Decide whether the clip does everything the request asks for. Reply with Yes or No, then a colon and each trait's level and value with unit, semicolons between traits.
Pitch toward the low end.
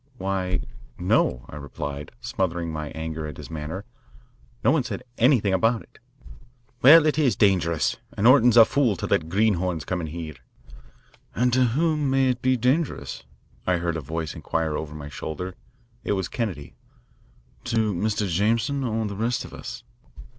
Yes: very low, 95 Hz